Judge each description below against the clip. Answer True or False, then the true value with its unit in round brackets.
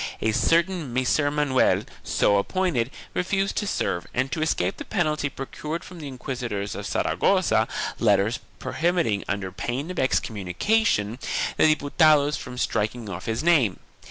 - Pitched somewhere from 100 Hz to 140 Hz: True (135 Hz)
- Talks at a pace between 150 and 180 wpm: False (140 wpm)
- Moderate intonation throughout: False (6.4 semitones)